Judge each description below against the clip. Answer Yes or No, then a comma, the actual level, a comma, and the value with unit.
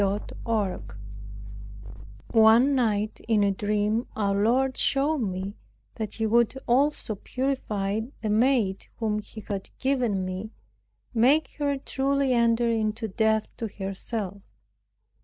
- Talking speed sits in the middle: No, slow, 120 wpm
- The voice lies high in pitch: Yes, high, 220 Hz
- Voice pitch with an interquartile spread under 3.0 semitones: No, average, 3.5 semitones